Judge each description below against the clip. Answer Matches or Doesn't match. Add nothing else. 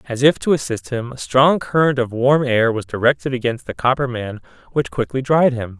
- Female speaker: Doesn't match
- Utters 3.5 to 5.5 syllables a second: Matches